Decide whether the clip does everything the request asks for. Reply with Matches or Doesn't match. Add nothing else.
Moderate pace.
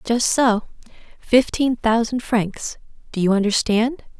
Doesn't match